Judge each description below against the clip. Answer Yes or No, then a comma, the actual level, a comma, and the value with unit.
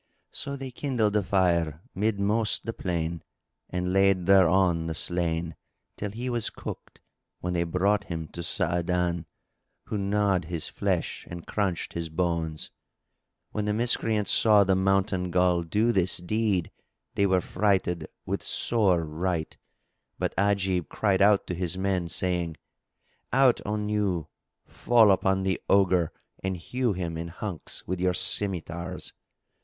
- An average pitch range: Yes, average, 3.1 semitones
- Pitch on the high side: No, very low, 95 Hz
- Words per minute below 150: Yes, average, 140 wpm